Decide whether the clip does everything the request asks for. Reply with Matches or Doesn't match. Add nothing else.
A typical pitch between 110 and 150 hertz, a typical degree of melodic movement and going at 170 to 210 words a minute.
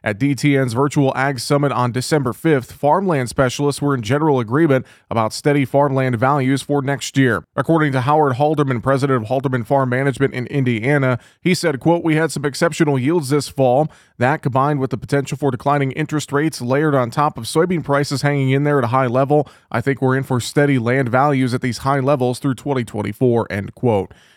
Doesn't match